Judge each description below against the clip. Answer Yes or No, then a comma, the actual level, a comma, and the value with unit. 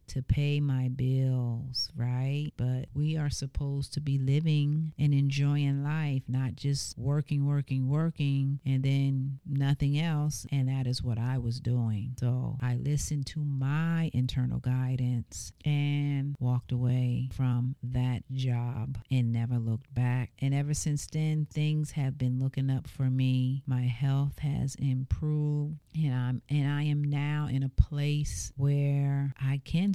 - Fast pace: No, average, 150 wpm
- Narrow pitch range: Yes, narrow, 2.3 semitones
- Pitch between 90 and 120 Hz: No, low, 135 Hz